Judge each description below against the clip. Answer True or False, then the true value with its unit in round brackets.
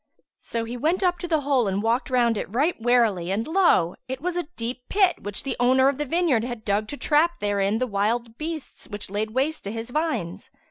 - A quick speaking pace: True (220 wpm)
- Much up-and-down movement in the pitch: True (5.9 semitones)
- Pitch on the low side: False (245 Hz)